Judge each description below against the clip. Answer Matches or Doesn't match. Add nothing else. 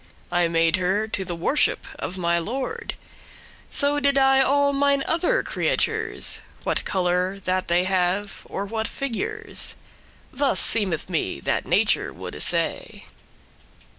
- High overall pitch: Matches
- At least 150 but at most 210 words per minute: Doesn't match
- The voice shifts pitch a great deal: Matches